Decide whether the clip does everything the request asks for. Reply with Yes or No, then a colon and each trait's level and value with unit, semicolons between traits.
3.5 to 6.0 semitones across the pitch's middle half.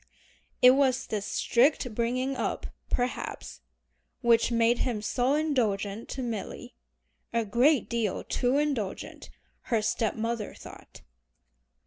No: average, 2.7 semitones